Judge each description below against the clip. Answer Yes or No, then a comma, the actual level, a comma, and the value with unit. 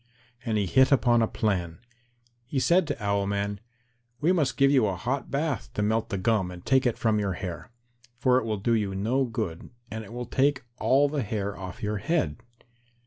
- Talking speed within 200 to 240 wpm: Yes, fast, 205 wpm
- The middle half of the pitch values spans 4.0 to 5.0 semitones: Yes, average, 4.7 semitones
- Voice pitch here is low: Yes, low, 110 Hz